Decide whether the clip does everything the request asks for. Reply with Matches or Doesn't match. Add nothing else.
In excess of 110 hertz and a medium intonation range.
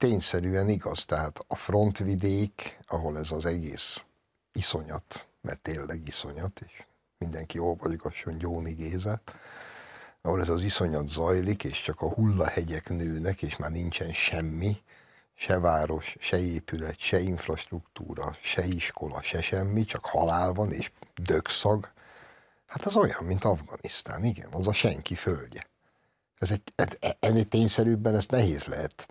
Doesn't match